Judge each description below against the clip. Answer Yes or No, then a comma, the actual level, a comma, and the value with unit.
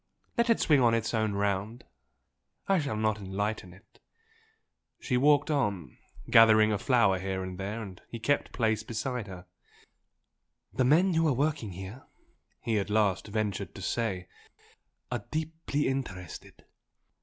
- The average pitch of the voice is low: Yes, low, 110 Hz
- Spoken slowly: No, average, 145 wpm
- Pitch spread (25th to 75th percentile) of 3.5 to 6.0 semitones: Yes, average, 5.1 semitones